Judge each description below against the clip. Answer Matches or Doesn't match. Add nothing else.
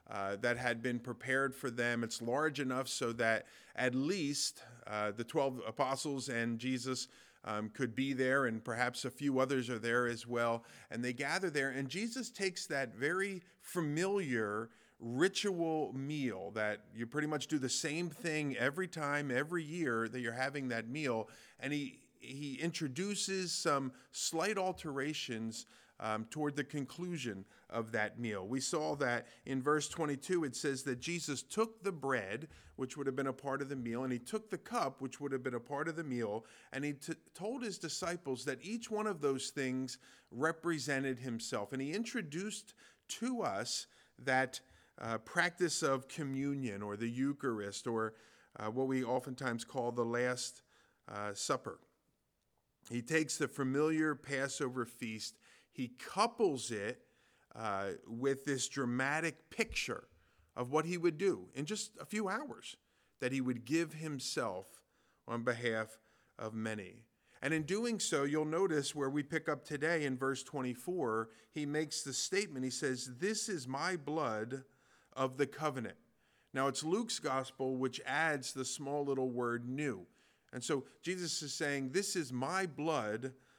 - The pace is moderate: Matches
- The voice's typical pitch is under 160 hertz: Matches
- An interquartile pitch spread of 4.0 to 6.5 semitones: Matches